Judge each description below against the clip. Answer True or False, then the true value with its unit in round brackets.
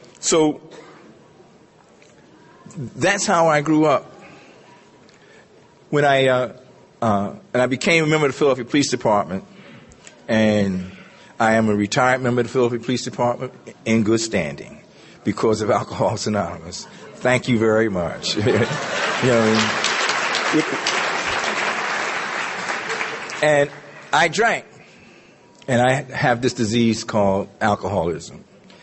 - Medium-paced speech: False (115 wpm)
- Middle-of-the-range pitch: False (120 Hz)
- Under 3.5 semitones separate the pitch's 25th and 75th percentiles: False (3.9 semitones)